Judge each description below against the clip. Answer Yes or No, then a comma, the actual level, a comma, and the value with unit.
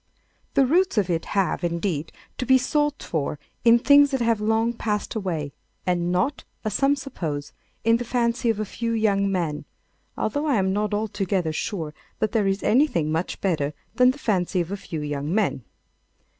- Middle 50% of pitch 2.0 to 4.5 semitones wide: No, wide, 5.5 semitones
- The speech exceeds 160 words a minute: Yes, average, 180 wpm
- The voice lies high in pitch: Yes, high, 205 Hz